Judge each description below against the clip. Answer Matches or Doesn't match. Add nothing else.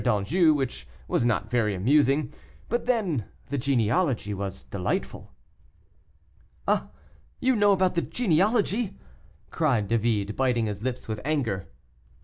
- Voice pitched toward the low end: Matches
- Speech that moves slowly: Matches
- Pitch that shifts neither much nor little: Doesn't match